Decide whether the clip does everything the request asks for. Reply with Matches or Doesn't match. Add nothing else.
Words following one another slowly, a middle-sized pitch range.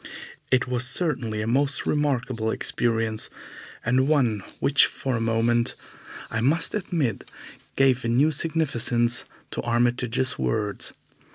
Matches